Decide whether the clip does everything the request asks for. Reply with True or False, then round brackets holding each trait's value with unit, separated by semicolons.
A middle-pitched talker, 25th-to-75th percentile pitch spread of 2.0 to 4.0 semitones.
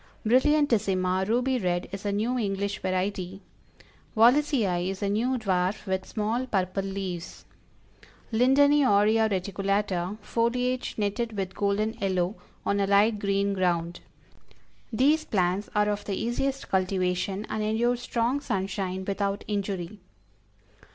False (200 Hz; 3.4 semitones)